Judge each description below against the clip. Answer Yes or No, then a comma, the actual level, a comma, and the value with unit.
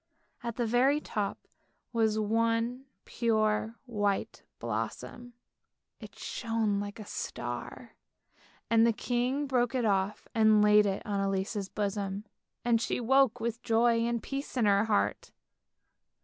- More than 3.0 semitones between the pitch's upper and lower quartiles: No, narrow, 2.6 semitones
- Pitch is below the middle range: No, high, 225 Hz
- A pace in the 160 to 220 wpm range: No, slow, 135 wpm